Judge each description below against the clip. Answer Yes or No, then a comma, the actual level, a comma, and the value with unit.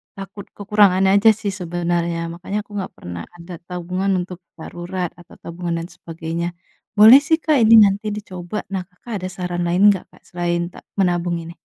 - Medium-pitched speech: Yes, medium, 180 Hz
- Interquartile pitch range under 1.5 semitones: No, average, 2.7 semitones